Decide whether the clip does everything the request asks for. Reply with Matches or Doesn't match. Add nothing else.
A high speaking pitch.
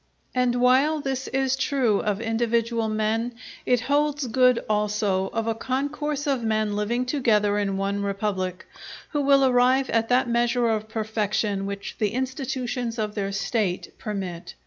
Matches